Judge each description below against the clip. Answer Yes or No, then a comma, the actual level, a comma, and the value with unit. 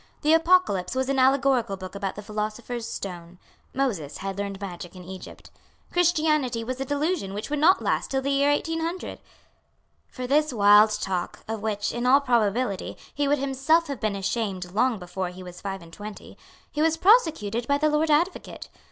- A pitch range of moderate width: No, wide, 6.5 semitones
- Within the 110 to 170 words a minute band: No, average, 180 wpm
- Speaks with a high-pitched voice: Yes, high, 240 Hz